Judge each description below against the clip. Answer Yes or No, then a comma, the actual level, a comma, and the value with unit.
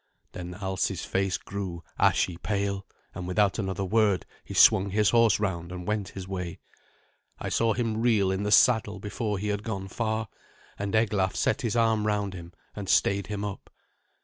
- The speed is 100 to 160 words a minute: No, average, 175 wpm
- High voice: No, low, 100 Hz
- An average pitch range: No, narrow, 2.2 semitones